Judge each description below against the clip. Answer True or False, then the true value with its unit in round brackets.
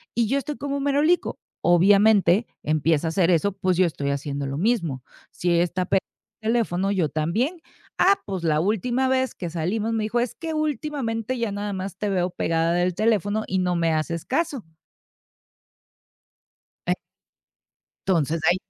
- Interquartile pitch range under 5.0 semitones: False (5.6 semitones)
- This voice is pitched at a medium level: False (195 Hz)